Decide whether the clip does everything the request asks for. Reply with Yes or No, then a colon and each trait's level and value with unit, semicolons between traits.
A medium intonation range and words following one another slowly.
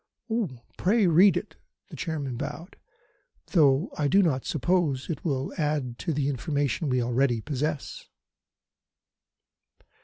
Yes: average, 3.6 semitones; slow, 120 wpm